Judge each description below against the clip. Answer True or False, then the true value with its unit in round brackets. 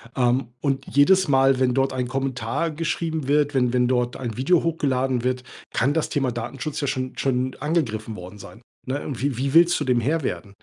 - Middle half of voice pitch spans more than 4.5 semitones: False (2.8 semitones)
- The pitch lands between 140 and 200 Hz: False (130 Hz)